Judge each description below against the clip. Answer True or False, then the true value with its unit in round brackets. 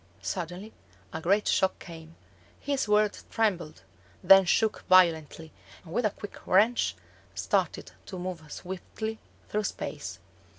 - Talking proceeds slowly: True (125 wpm)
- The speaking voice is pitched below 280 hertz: True (190 Hz)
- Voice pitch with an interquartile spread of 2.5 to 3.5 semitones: False (4.0 semitones)